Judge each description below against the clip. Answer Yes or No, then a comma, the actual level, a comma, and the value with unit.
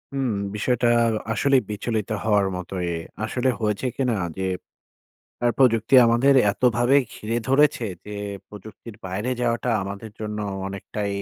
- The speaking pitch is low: Yes, low, 110 Hz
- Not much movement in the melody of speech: No, average, 3.3 semitones